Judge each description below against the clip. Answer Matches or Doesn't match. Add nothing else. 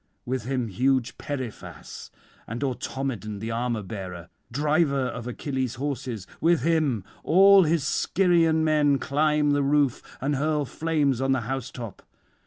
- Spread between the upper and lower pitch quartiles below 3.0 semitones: Doesn't match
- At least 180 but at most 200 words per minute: Doesn't match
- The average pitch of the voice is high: Doesn't match